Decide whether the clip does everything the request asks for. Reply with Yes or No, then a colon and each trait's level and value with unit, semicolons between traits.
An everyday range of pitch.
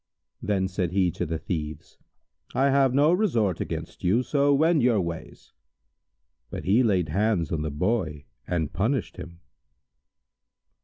No: wide, 7.3 semitones